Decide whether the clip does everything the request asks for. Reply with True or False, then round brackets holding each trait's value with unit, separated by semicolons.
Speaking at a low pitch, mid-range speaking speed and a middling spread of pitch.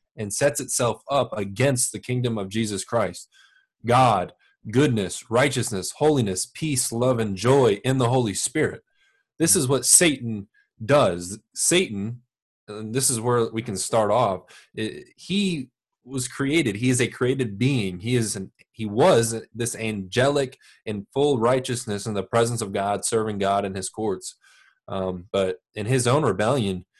True (120 Hz; 155 wpm; 4.5 semitones)